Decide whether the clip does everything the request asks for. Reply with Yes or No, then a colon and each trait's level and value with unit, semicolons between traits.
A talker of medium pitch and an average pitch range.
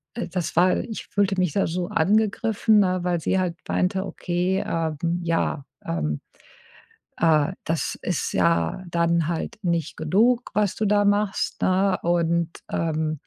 Yes: medium, 175 Hz; average, 3.3 semitones